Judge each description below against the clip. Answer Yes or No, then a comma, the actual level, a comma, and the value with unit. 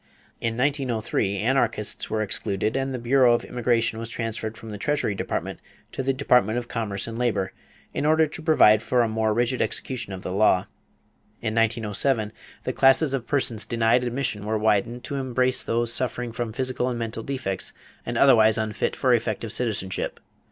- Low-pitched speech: Yes, low, 115 Hz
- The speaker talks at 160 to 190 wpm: Yes, average, 175 wpm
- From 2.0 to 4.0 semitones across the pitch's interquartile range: Yes, average, 2.8 semitones